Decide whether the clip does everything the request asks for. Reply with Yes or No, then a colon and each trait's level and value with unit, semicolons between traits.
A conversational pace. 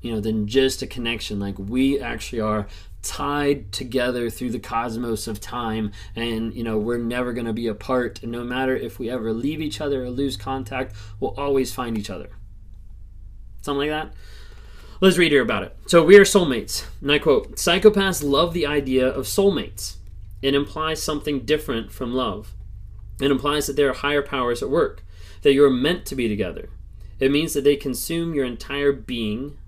Yes: average, 185 wpm